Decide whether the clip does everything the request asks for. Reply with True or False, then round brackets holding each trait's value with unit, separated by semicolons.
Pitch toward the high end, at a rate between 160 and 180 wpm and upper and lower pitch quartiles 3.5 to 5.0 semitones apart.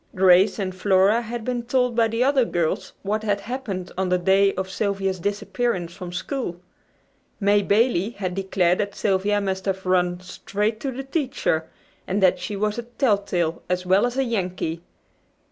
True (200 Hz; 175 wpm; 3.8 semitones)